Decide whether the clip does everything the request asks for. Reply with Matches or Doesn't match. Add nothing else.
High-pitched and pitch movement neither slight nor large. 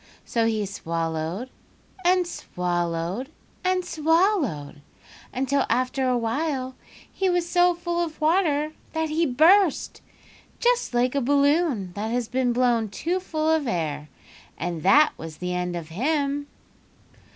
Doesn't match